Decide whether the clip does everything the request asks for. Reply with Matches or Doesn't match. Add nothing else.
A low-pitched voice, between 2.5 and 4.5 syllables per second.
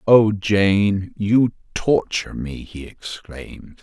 Matches